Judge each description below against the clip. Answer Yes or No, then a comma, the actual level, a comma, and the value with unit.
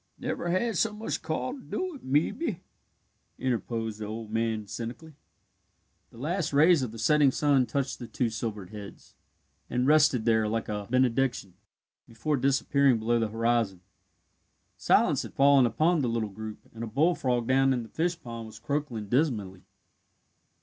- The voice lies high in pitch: No, low, 125 Hz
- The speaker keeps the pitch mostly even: No, average, 4.9 semitones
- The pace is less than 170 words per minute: Yes, average, 155 wpm